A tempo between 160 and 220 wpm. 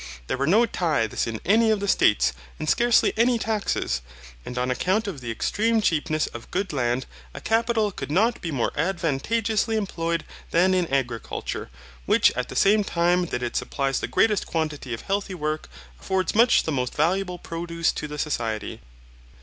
Yes: average, 175 wpm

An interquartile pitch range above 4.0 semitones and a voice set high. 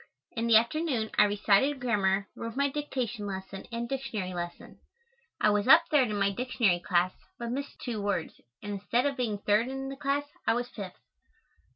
Yes: average, 4.8 semitones; high, 230 Hz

